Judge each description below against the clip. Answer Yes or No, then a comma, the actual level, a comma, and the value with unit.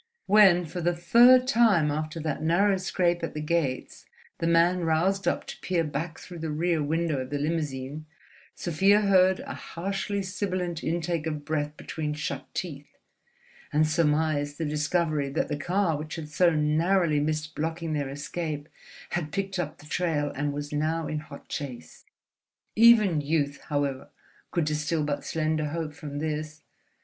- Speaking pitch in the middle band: Yes, medium, 160 Hz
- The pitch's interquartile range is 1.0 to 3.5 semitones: Yes, average, 2.7 semitones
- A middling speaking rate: Yes, average, 160 wpm